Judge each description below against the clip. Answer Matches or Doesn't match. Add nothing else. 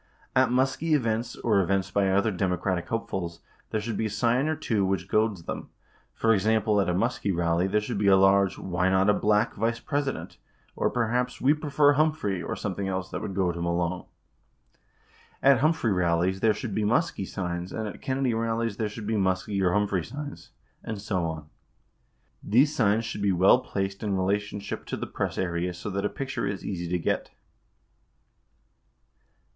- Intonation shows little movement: Doesn't match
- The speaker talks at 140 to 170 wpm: Doesn't match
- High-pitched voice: Doesn't match